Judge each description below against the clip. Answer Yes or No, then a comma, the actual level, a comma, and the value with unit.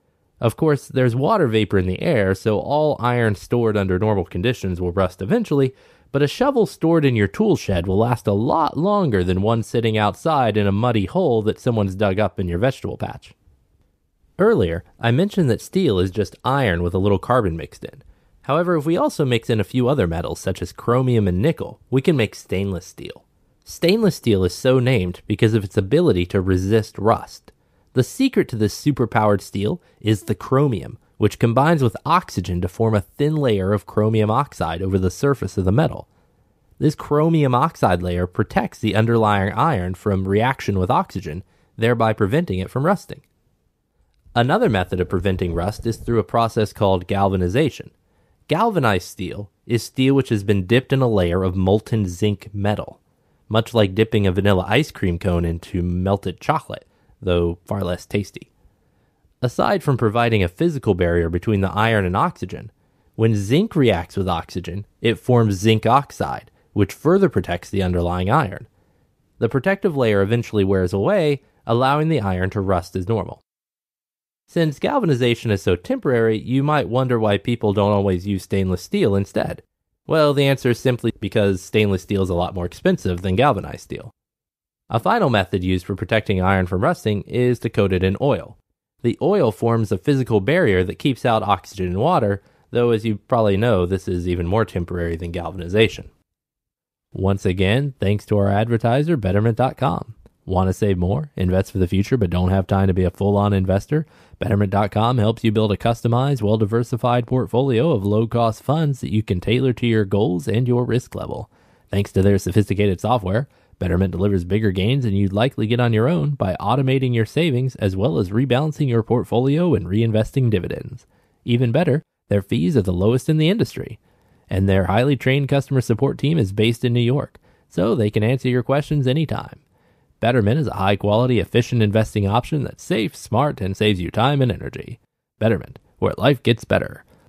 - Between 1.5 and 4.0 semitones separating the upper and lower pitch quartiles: No, average, 4.7 semitones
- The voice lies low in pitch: Yes, low, 110 Hz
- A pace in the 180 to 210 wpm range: Yes, average, 185 wpm